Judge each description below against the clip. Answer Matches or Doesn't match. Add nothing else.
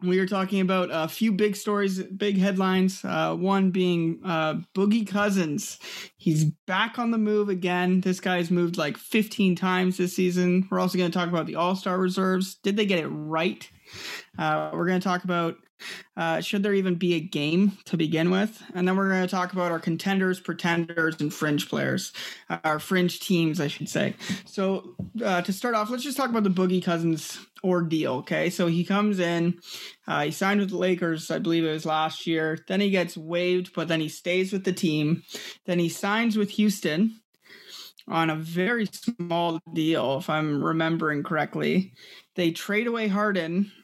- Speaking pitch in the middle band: Matches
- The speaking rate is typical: Matches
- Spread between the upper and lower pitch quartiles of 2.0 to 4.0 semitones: Matches